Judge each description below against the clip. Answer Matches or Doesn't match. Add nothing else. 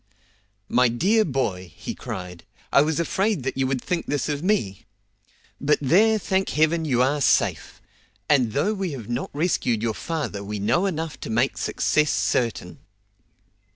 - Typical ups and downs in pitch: Doesn't match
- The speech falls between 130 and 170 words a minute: Matches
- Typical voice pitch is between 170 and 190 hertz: Doesn't match